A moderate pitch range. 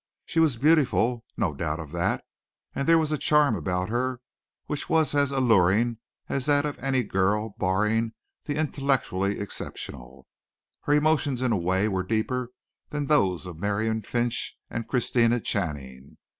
No: wide, 6.6 semitones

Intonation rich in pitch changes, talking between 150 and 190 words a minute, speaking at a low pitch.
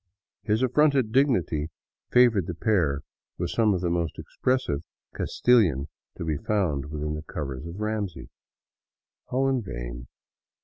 No: wide, 7.8 semitones; slow, 135 wpm; very low, 90 Hz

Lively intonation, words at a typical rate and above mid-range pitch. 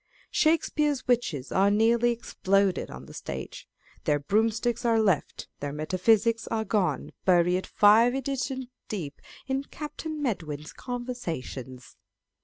No: wide, 5.7 semitones; slow, 120 wpm; high, 220 Hz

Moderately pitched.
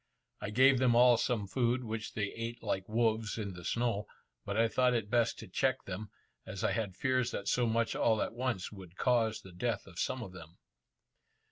No: low, 115 Hz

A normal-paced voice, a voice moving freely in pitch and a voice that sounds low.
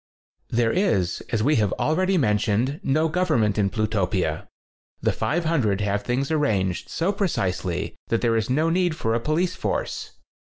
Yes: average, 165 wpm; wide, 7.6 semitones; low, 120 Hz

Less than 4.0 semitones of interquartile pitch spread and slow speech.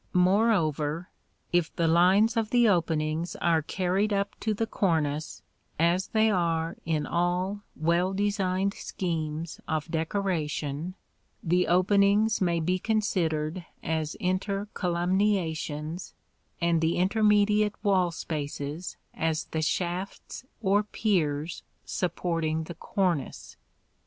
Yes: average, 3.6 semitones; slow, 105 wpm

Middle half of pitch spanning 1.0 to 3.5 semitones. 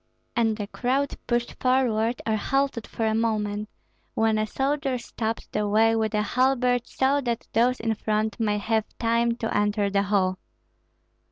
Yes: narrow, 2.6 semitones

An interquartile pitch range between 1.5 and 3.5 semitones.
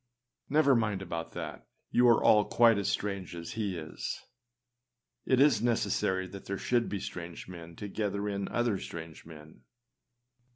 No: average, 4.7 semitones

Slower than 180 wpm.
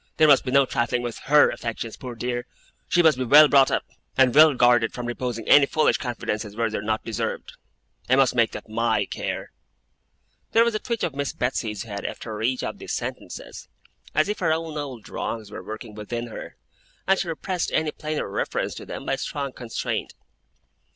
No: average, 200 wpm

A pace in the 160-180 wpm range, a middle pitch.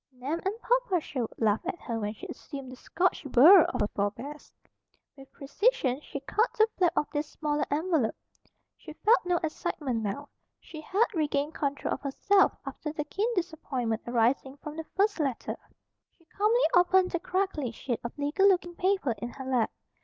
No: average, 175 wpm; very high, 300 Hz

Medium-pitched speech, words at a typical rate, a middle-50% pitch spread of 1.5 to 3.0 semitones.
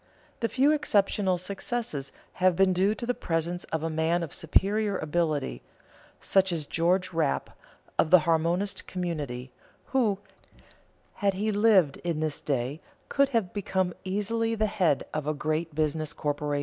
No: medium, 175 Hz; average, 150 wpm; average, 4.5 semitones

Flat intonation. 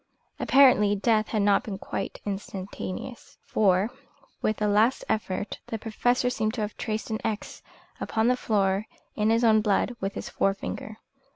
Yes: narrow, 1.8 semitones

